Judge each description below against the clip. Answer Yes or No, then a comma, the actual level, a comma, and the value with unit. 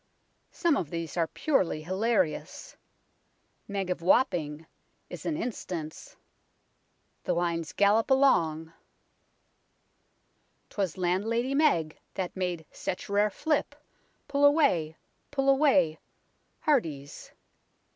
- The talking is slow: Yes, slow, 105 wpm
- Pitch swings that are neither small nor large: No, wide, 8.3 semitones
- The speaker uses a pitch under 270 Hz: Yes, high, 190 Hz